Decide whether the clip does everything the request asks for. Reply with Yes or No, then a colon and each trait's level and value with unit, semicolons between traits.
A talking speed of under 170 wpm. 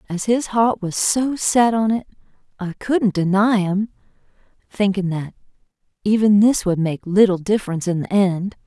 Yes: average, 160 wpm